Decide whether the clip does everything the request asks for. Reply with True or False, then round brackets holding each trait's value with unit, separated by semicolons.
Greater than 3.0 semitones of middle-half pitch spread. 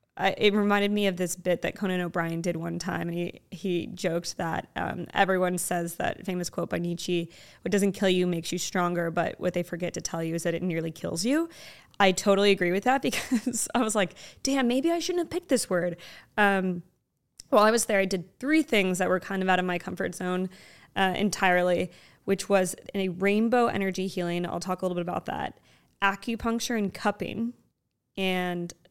False (2.6 semitones)